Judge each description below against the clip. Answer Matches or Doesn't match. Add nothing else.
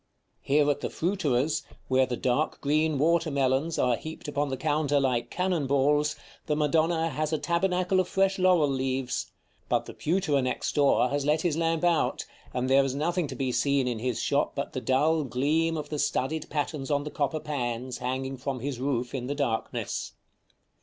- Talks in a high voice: Doesn't match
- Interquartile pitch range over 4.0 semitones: Doesn't match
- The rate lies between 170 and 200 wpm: Matches